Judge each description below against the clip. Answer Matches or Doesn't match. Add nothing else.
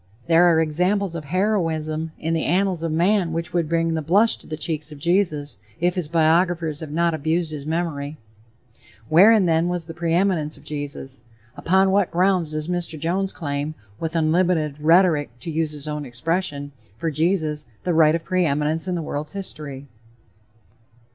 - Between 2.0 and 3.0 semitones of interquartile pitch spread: Matches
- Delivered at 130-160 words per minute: Doesn't match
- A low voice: Doesn't match